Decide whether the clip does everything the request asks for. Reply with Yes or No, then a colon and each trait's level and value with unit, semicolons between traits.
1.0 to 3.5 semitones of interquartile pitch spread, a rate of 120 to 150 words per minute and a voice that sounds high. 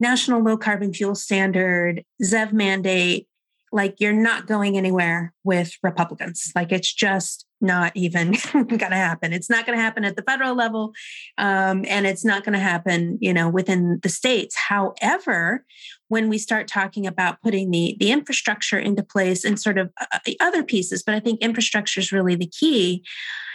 No: average, 3.0 semitones; average, 175 wpm; high, 200 Hz